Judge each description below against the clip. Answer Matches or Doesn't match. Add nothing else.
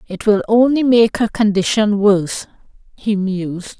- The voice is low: Doesn't match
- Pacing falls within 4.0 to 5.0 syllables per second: Matches